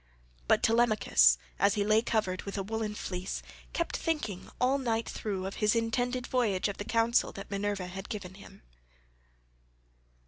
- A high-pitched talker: Yes, high, 210 Hz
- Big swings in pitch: No, average, 2.9 semitones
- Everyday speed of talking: Yes, average, 170 wpm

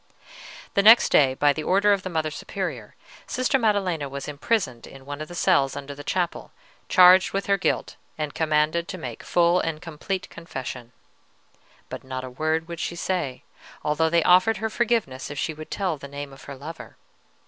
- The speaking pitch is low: No, medium, 160 Hz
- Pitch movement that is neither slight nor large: Yes, average, 4.6 semitones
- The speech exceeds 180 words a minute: Yes, average, 190 wpm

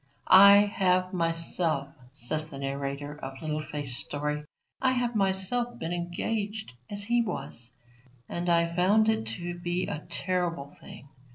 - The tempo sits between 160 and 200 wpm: No, average, 145 wpm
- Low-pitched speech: No, medium, 175 Hz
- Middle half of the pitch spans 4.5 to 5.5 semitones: Yes, average, 5.1 semitones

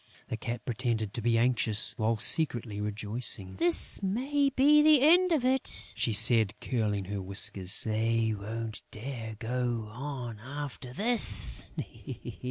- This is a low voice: Yes, low, 115 Hz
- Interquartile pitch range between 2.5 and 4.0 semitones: No, average, 5.2 semitones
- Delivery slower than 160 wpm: Yes, average, 140 wpm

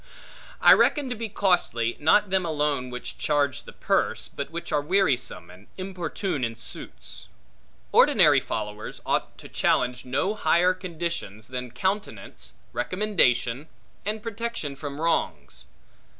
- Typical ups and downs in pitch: No, wide, 7.4 semitones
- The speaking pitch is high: No, medium, 150 Hz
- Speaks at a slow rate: Yes, slow, 130 wpm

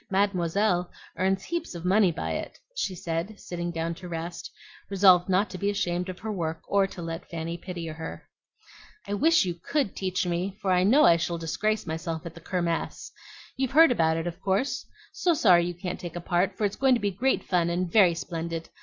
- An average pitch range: Yes, average, 3.0 semitones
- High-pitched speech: No, medium, 180 Hz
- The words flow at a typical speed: No, fast, 210 wpm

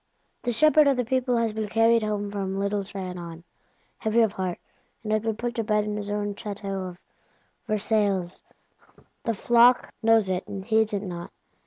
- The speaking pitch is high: Yes, high, 210 Hz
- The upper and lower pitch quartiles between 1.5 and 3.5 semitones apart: Yes, narrow, 2.5 semitones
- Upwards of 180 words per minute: No, average, 175 wpm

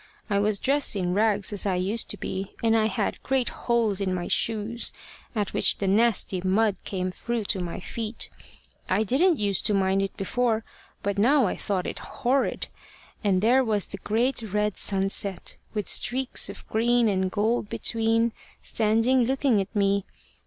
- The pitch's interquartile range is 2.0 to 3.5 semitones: Yes, average, 3.0 semitones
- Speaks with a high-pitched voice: Yes, high, 210 Hz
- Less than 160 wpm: No, average, 175 wpm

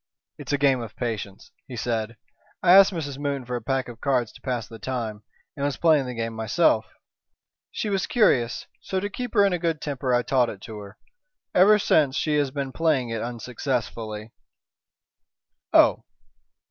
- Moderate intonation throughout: Yes, average, 4.6 semitones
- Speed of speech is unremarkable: Yes, average, 185 wpm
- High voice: No, low, 130 Hz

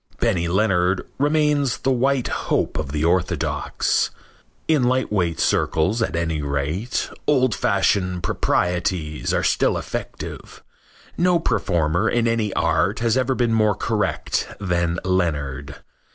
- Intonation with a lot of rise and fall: Yes, wide, 6.2 semitones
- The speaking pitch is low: Yes, very low, 95 Hz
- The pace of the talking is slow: Yes, slow, 125 wpm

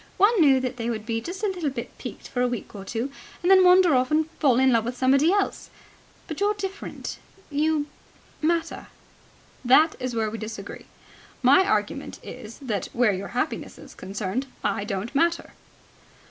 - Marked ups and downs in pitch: Yes, wide, 6.5 semitones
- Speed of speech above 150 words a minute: Yes, average, 180 wpm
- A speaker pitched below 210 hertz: No, very high, 260 Hz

